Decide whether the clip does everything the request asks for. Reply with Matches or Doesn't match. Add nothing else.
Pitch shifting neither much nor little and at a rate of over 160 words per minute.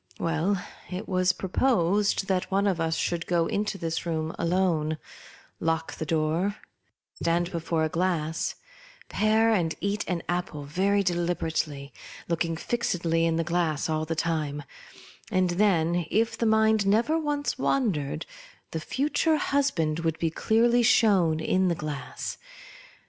Doesn't match